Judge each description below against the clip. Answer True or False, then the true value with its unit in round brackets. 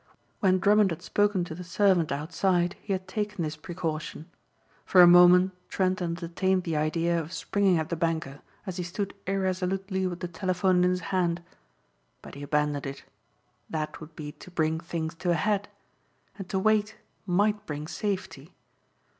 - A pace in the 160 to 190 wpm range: True (170 wpm)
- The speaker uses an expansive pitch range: False (2.7 semitones)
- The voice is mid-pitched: True (180 Hz)